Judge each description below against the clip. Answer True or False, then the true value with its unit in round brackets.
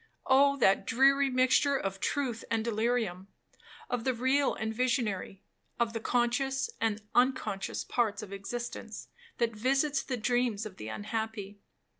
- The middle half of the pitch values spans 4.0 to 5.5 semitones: False (3.5 semitones)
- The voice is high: True (235 Hz)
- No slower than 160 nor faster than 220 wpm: False (140 wpm)